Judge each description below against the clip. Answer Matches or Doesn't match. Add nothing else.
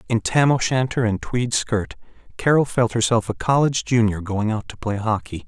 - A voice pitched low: Matches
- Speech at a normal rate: Matches